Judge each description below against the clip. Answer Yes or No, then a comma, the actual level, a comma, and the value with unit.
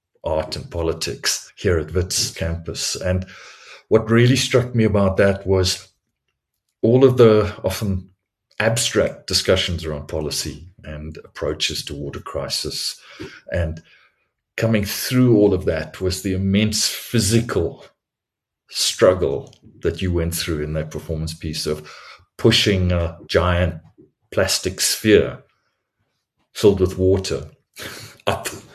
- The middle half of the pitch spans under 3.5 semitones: No, average, 4.8 semitones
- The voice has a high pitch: No, very low, 95 Hz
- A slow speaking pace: Yes, slow, 120 wpm